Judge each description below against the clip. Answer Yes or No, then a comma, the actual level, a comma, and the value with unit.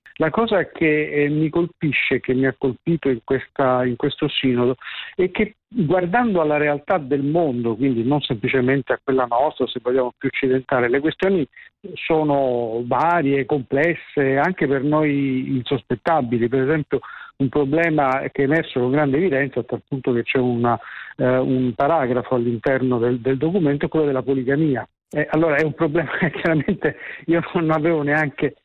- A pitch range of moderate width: Yes, average, 3.4 semitones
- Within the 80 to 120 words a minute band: No, average, 165 wpm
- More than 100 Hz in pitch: Yes, medium, 140 Hz